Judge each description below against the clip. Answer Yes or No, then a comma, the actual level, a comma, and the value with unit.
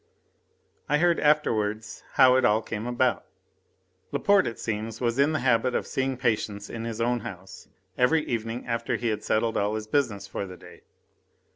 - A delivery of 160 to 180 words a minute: Yes, average, 175 wpm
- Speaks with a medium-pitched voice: No, low, 115 Hz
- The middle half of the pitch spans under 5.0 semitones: Yes, average, 3.1 semitones